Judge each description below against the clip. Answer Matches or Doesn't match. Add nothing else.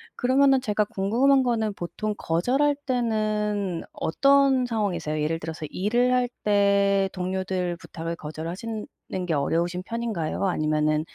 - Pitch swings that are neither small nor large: Doesn't match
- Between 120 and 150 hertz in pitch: Doesn't match